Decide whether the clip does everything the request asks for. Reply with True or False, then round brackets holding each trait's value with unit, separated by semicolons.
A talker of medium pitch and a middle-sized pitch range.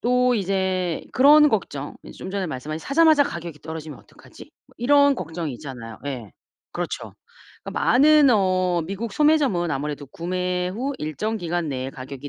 False (180 Hz; 8.4 semitones)